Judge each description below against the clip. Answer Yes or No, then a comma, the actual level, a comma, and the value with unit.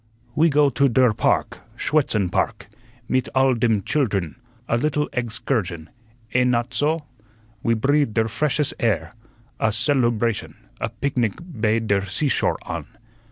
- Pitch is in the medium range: No, low, 120 Hz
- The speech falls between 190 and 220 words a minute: No, average, 140 wpm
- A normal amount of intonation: Yes, average, 4.3 semitones